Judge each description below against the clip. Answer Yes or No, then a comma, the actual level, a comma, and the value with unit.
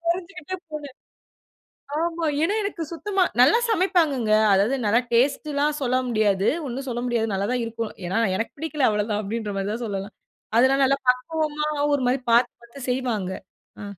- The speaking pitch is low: No, very high, 255 Hz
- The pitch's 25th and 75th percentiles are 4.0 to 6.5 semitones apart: Yes, wide, 5.4 semitones